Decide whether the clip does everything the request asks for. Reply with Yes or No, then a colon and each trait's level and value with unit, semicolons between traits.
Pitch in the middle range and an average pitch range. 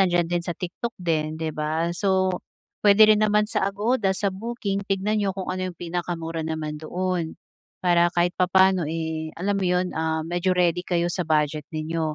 Yes: medium, 175 Hz; average, 3.0 semitones